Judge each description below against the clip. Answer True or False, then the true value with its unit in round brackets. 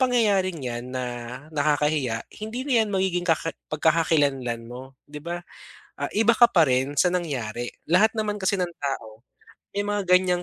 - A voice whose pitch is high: False (165 Hz)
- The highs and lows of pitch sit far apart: True (6.7 semitones)